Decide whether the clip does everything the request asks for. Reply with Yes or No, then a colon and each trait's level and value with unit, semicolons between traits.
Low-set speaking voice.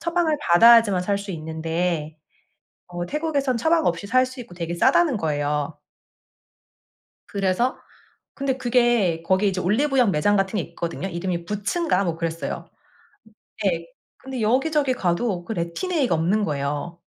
No: high, 195 Hz